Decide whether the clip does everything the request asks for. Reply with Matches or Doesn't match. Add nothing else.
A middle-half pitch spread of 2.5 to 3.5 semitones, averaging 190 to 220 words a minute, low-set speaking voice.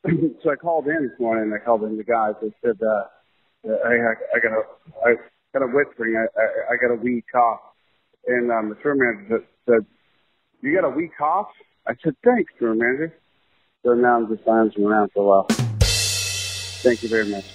Matches